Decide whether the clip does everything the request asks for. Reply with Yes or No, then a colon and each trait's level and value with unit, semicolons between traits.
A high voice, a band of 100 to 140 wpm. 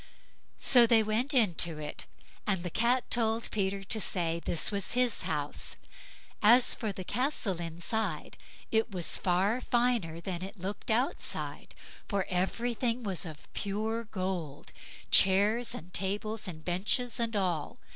Yes: high, 200 Hz; slow, 135 wpm